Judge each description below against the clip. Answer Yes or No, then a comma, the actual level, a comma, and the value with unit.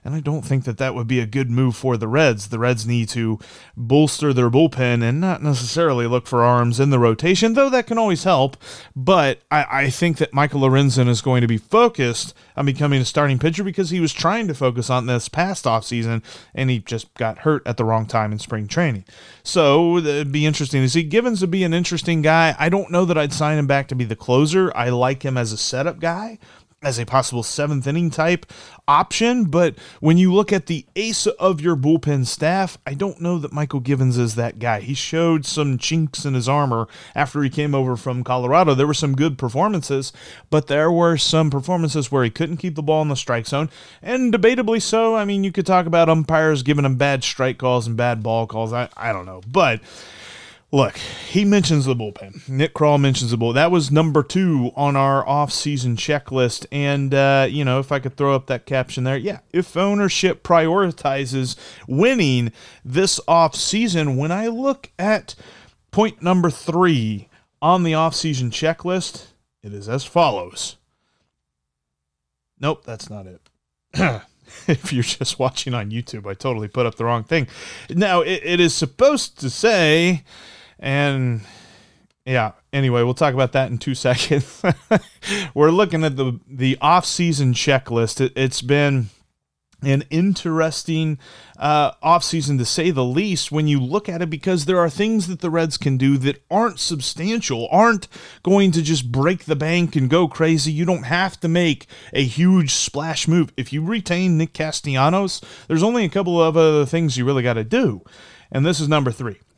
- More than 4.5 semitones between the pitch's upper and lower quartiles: Yes, average, 5.1 semitones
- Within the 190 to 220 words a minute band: Yes, average, 195 wpm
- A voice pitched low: No, medium, 145 Hz